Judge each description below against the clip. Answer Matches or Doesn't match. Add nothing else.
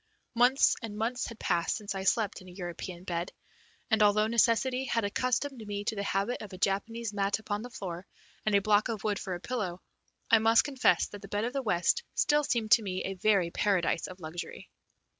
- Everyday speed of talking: Doesn't match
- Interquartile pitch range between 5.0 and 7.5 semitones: Doesn't match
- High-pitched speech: Matches